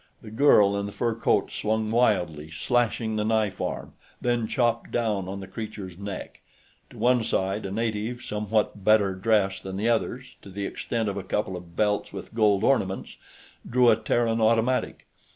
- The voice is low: Yes, low, 110 Hz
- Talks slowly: No, average, 175 wpm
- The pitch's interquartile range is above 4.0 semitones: No, average, 2.8 semitones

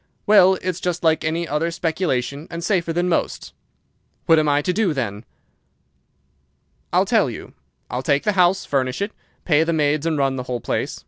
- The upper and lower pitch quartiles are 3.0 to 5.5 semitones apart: Yes, average, 3.8 semitones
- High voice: No, medium, 160 Hz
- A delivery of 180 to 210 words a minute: Yes, average, 185 wpm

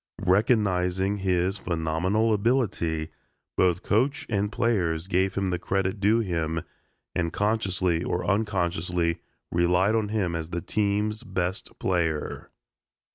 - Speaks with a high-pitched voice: No, very low, 95 Hz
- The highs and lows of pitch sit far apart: No, average, 3.2 semitones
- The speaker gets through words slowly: Yes, slow, 120 wpm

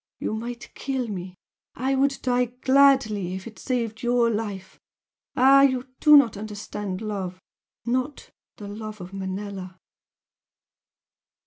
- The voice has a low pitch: No, high, 220 Hz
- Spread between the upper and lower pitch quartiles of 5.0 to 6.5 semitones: No, average, 4.3 semitones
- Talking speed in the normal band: No, slow, 125 wpm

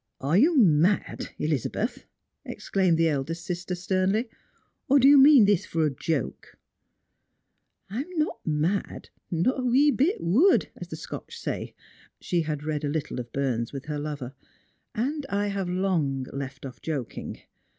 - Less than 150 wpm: No, average, 185 wpm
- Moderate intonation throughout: No, wide, 7.0 semitones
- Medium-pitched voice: Yes, medium, 175 Hz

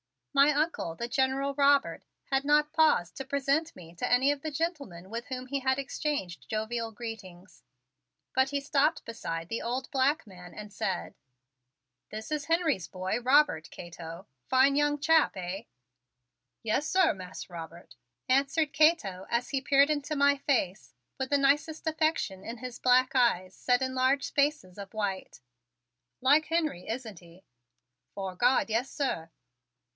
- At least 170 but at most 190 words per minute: No, average, 155 wpm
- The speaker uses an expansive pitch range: Yes, wide, 6.6 semitones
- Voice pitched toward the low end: No, very high, 260 Hz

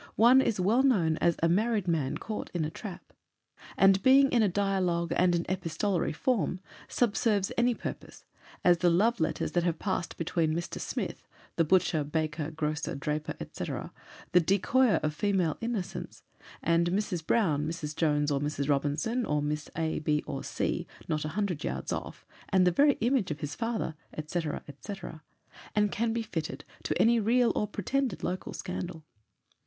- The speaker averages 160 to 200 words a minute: Yes, average, 170 wpm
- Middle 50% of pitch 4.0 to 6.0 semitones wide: Yes, average, 5.2 semitones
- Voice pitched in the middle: Yes, medium, 180 Hz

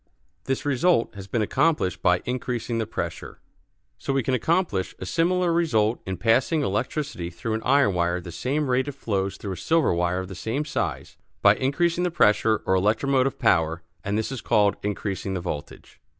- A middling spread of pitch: No, wide, 6.8 semitones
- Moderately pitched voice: No, low, 115 Hz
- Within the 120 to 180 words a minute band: No, average, 190 wpm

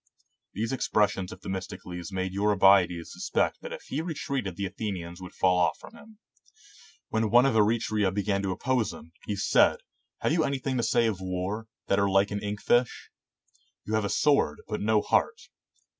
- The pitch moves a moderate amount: Yes, average, 3.4 semitones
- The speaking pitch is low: Yes, low, 105 Hz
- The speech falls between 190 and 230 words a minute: Yes, average, 195 wpm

